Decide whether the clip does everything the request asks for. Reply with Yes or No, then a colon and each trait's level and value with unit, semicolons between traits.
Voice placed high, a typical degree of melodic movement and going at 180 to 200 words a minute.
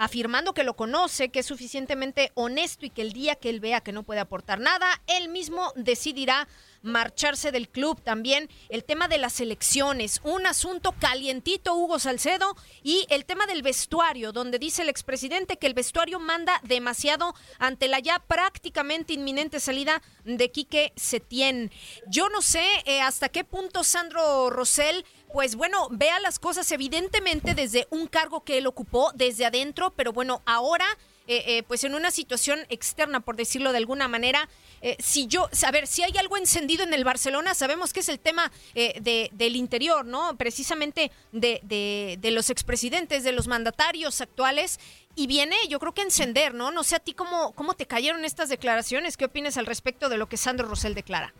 Yes: very high, 285 Hz; average, 5.0 semitones; average, 185 wpm